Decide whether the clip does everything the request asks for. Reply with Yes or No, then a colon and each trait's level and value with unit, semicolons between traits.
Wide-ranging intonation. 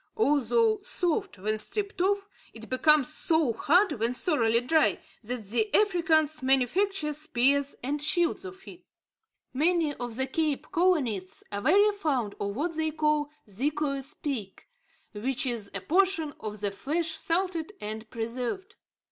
Yes: wide, 6.4 semitones